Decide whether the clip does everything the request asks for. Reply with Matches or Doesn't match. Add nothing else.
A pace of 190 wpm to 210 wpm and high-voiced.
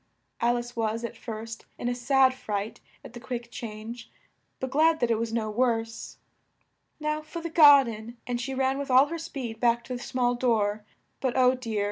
Matches